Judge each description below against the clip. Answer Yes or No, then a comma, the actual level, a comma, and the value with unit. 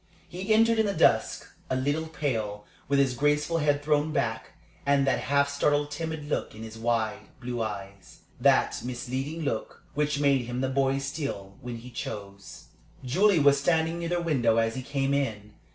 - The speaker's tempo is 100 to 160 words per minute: No, average, 180 wpm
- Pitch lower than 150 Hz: Yes, medium, 140 Hz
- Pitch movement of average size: Yes, average, 4.1 semitones